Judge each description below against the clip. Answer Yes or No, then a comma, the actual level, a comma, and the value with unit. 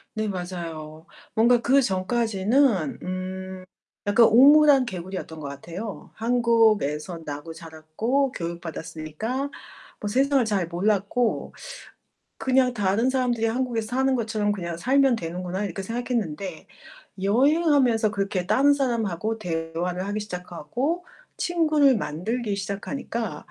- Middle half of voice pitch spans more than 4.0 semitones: Yes, wide, 5.6 semitones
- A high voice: Yes, high, 210 Hz